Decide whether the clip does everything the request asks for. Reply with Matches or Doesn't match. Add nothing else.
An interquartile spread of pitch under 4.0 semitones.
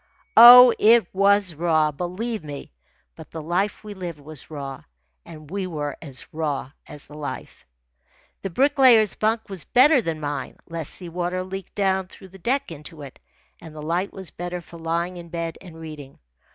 Doesn't match